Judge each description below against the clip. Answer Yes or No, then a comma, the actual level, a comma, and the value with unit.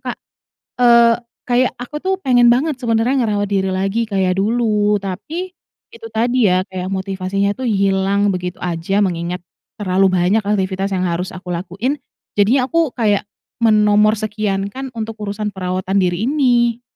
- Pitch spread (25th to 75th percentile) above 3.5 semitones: Yes, average, 3.9 semitones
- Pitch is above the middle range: Yes, high, 205 Hz